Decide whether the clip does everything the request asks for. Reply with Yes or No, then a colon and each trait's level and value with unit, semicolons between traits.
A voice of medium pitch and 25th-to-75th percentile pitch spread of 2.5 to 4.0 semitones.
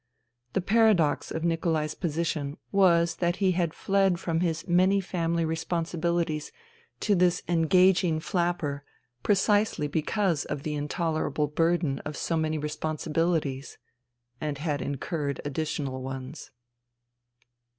Yes: medium, 165 Hz; average, 2.8 semitones